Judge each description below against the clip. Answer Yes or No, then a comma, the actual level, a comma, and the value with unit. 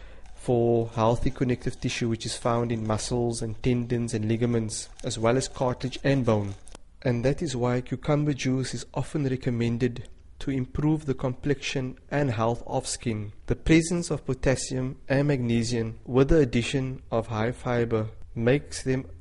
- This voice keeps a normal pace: Yes, average, 155 wpm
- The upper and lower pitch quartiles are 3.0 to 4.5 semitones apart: No, narrow, 2.6 semitones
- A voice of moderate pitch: No, low, 125 Hz